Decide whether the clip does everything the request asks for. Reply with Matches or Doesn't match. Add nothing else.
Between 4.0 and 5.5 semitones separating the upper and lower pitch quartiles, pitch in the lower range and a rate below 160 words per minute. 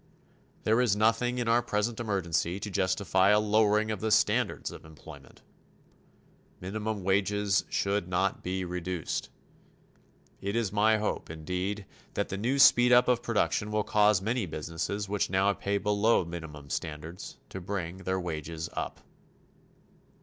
Doesn't match